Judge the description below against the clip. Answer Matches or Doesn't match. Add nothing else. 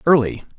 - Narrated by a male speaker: Matches